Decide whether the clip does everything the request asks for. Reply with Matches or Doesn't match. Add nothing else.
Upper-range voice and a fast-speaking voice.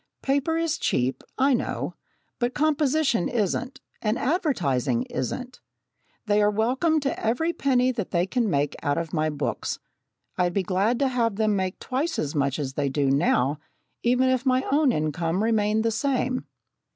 Doesn't match